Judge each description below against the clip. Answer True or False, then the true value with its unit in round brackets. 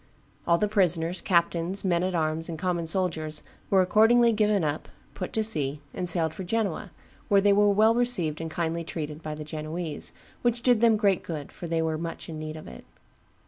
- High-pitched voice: False (170 Hz)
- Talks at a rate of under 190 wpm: False (200 wpm)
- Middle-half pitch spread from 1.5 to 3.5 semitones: False (4.2 semitones)